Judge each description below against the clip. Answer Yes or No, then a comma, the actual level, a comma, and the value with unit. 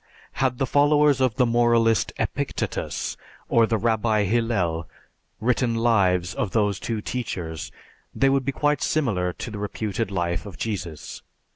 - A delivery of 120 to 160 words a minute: Yes, average, 145 wpm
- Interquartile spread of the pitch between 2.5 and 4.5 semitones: Yes, average, 4.2 semitones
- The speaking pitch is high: No, low, 115 Hz